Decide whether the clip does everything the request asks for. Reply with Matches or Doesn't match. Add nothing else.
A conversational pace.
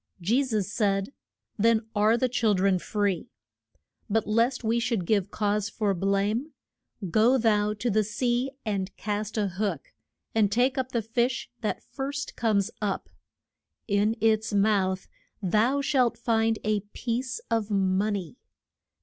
Matches